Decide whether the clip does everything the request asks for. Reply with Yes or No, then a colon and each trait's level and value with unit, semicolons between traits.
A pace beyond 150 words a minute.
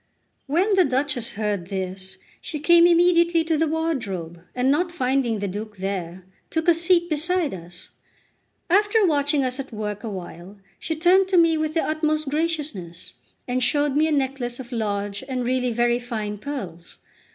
Yes: average, 170 wpm